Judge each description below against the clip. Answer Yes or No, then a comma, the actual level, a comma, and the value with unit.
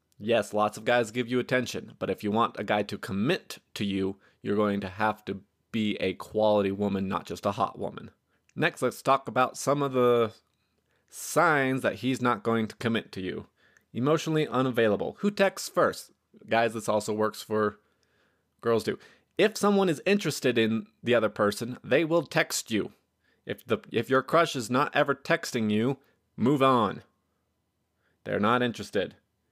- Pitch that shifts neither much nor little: Yes, average, 4.0 semitones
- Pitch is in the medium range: No, low, 115 Hz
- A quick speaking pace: No, average, 175 wpm